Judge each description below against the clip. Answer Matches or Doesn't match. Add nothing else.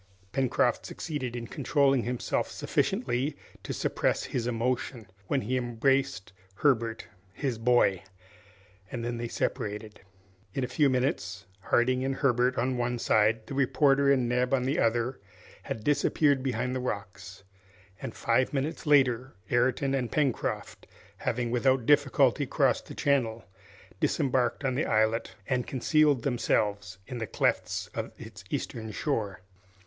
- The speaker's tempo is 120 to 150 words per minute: Matches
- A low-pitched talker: Matches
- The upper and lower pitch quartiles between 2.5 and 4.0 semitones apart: Matches